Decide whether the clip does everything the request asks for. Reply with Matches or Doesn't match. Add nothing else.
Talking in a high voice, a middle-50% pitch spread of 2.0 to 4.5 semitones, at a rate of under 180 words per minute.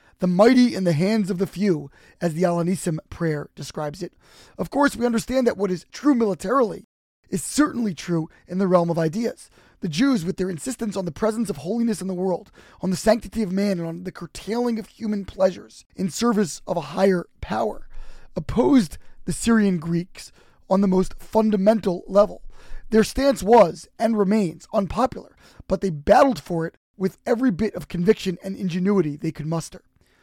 Doesn't match